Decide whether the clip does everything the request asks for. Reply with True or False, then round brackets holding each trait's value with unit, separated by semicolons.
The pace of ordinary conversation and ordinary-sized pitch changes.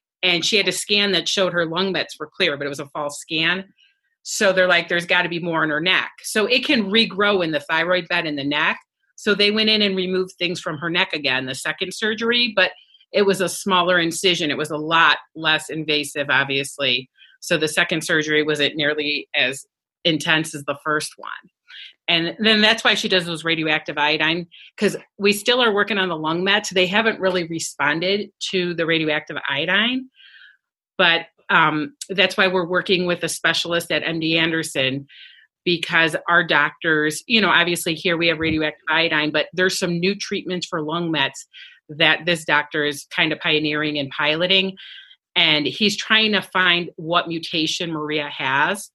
True (190 wpm; 3.6 semitones)